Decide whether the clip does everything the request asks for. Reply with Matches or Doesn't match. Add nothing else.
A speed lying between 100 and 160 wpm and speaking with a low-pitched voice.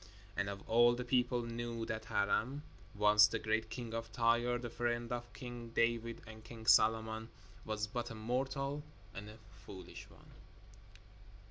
Matches